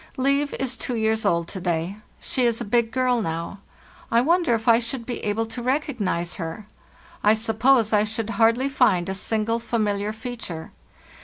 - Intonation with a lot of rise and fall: No, average, 3.2 semitones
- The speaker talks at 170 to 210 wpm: Yes, average, 180 wpm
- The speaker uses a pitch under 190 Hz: No, high, 225 Hz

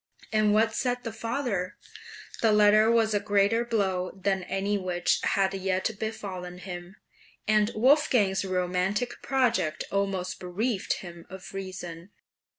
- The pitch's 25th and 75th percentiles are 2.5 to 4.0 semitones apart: Yes, average, 3.1 semitones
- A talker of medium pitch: No, high, 200 Hz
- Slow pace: Yes, slow, 130 wpm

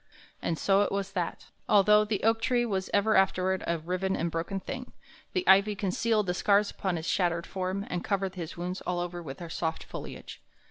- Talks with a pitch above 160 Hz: Yes, high, 190 Hz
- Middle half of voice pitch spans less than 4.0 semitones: Yes, narrow, 2.6 semitones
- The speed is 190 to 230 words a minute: Yes, average, 200 wpm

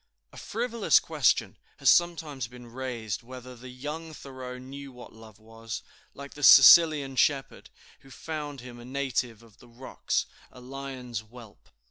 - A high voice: No, low, 130 Hz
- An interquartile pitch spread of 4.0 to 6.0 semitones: No, average, 3.0 semitones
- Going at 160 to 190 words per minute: No, average, 150 wpm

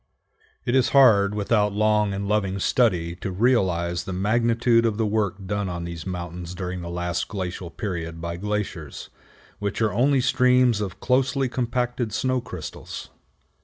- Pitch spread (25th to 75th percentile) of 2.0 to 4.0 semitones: No, average, 4.8 semitones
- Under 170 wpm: Yes, average, 155 wpm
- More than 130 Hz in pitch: No, low, 100 Hz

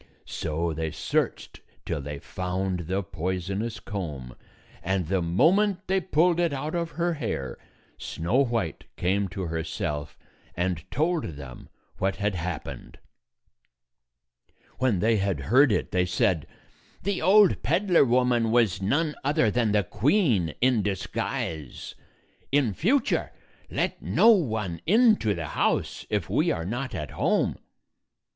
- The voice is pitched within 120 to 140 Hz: No, low, 100 Hz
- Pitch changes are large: Yes, wide, 9.0 semitones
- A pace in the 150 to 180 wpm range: No, slow, 135 wpm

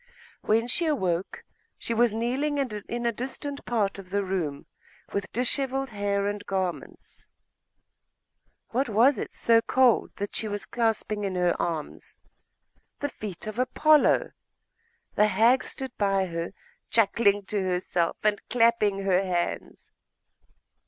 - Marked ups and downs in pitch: No, average, 3.8 semitones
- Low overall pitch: No, high, 210 Hz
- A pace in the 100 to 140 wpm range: Yes, slow, 135 wpm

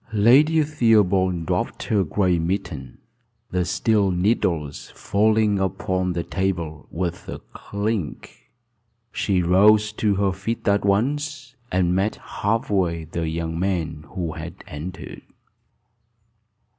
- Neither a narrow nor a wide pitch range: Yes, average, 3.8 semitones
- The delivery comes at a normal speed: No, slow, 120 wpm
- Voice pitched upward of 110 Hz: No, very low, 95 Hz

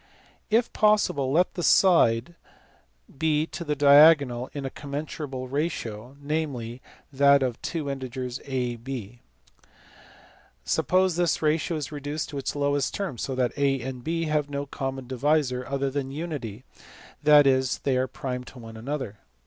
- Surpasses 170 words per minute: No, average, 155 wpm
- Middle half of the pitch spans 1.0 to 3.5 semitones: Yes, average, 3.0 semitones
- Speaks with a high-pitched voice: No, medium, 140 Hz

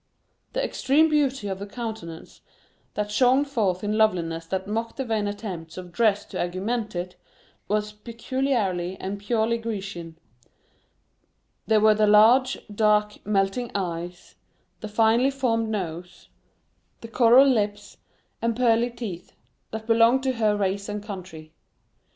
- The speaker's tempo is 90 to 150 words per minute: Yes, slow, 135 wpm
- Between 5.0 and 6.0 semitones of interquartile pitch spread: No, average, 3.4 semitones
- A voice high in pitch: Yes, high, 210 Hz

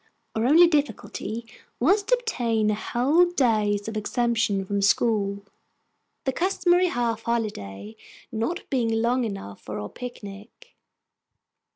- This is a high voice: Yes, high, 230 Hz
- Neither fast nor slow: No, slow, 115 wpm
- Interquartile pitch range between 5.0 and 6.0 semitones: Yes, average, 5.3 semitones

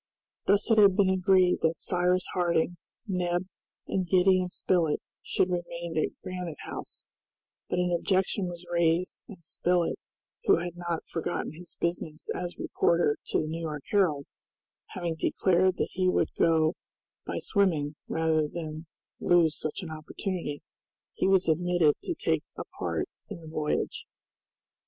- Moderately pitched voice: Yes, medium, 175 Hz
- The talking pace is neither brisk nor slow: Yes, average, 145 wpm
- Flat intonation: Yes, narrow, 2.2 semitones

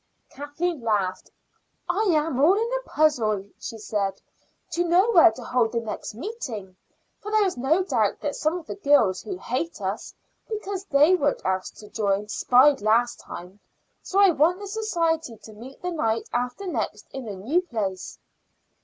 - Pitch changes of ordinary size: No, wide, 8.5 semitones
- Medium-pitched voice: No, very high, 280 Hz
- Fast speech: No, average, 175 wpm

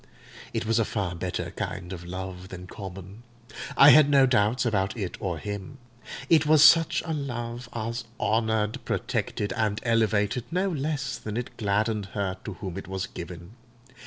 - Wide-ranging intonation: No, average, 4.6 semitones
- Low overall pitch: Yes, low, 110 Hz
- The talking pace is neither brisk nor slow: Yes, average, 165 wpm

